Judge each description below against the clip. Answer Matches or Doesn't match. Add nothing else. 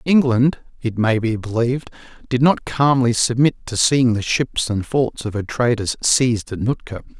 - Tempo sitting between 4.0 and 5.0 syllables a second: Matches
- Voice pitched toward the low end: Matches